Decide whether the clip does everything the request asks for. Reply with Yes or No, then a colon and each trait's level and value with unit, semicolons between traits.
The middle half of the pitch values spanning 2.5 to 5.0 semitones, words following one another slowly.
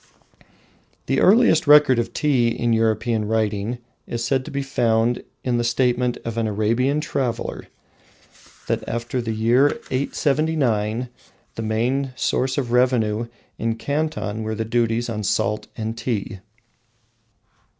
Yes: average, 2.8 semitones; slow, 130 wpm